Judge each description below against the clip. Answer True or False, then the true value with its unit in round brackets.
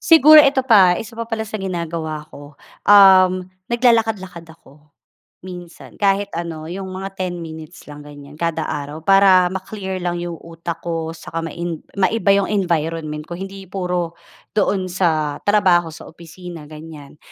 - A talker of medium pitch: True (175 Hz)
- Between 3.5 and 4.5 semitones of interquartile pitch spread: False (3.1 semitones)